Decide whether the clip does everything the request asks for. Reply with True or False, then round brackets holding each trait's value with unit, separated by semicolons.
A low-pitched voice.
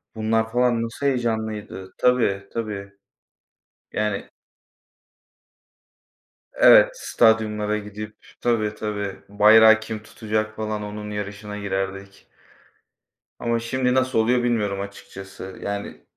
True (105 Hz)